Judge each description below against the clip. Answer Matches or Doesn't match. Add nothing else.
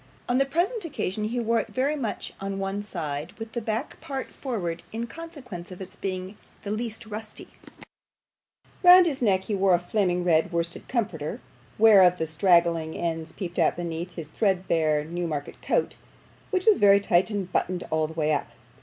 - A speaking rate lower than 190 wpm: Matches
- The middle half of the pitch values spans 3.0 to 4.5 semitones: Doesn't match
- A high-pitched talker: Matches